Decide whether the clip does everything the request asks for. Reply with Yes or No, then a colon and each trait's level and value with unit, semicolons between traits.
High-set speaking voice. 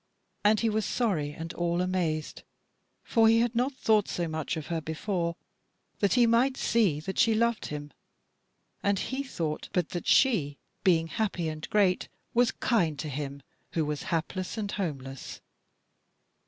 No: medium, 180 Hz